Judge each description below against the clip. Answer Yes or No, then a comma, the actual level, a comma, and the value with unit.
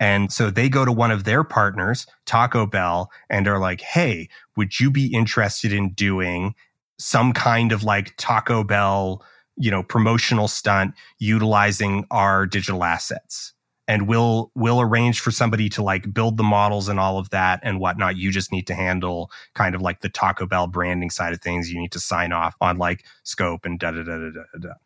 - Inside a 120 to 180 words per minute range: No, average, 200 wpm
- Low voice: Yes, low, 100 Hz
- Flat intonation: No, average, 3.7 semitones